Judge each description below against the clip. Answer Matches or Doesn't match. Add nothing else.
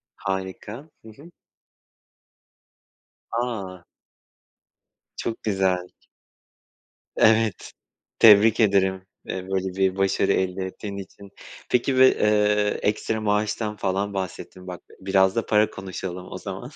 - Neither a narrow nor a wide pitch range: Doesn't match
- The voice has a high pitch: Doesn't match